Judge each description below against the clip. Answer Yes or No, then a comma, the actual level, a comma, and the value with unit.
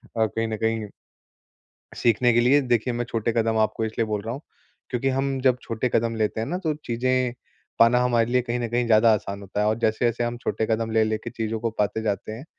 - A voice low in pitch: Yes, low, 115 Hz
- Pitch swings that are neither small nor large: No, narrow, 1.8 semitones